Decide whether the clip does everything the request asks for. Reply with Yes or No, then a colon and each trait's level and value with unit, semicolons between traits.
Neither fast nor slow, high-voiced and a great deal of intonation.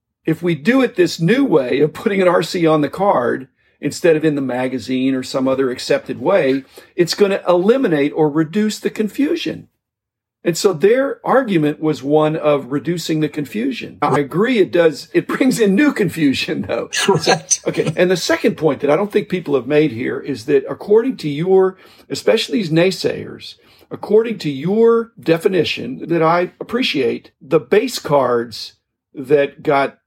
No: average, 170 wpm; medium, 170 Hz; wide, 6.4 semitones